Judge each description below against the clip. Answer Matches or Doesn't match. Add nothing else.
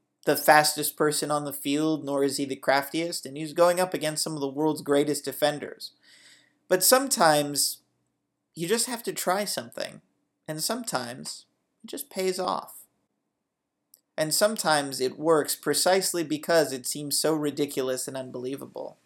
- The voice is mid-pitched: Matches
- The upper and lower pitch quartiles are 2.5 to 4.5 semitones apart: Matches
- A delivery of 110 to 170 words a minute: Matches